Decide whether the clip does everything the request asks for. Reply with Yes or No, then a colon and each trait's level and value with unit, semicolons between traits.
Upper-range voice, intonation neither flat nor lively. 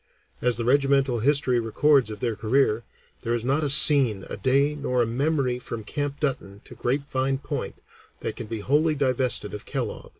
No: low, 130 Hz; average, 3.2 semitones